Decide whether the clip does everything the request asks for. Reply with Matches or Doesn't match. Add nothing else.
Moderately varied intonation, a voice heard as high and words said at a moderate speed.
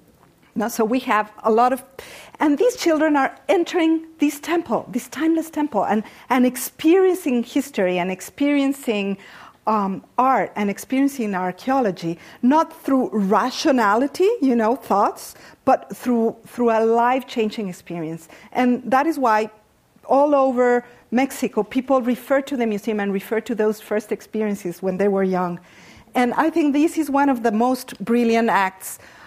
Matches